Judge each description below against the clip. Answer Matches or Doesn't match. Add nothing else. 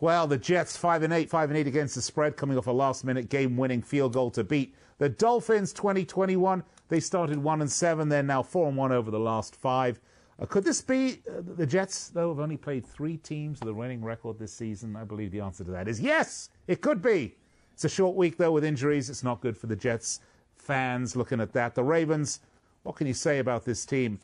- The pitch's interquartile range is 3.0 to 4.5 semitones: Doesn't match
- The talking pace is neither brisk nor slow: Doesn't match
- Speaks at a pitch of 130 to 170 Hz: Matches